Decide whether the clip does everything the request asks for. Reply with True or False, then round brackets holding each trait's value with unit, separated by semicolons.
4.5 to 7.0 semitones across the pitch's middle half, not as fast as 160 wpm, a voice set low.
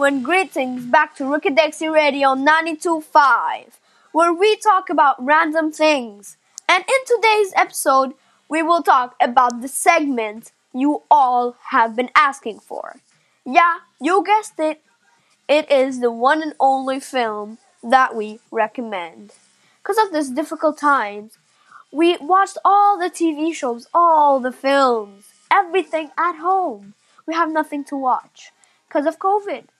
False (5.0 semitones; 135 wpm; 305 Hz)